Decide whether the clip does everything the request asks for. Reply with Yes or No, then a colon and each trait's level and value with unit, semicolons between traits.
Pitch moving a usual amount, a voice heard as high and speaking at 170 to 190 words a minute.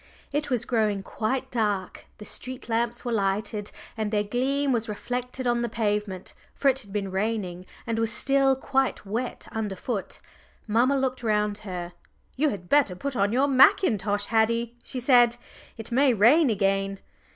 No: average, 3.7 semitones; high, 225 Hz; average, 160 wpm